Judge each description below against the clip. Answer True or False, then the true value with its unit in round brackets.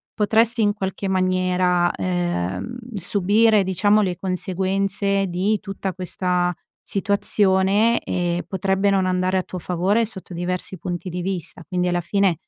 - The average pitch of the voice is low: False (190 Hz)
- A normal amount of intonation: False (1.9 semitones)